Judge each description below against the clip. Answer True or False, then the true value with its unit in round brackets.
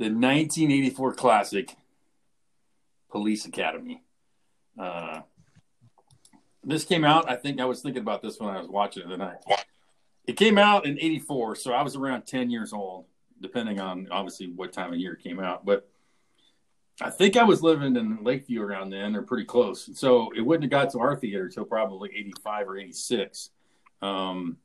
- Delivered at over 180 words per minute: False (175 wpm)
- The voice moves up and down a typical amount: False (7.8 semitones)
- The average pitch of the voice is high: False (130 Hz)